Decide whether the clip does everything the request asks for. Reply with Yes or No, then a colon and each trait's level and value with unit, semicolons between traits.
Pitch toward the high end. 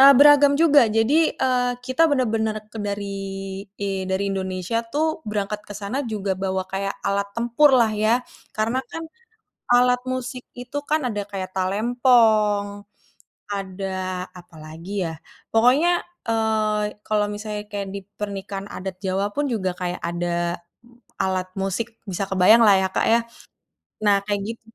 Yes: high, 210 Hz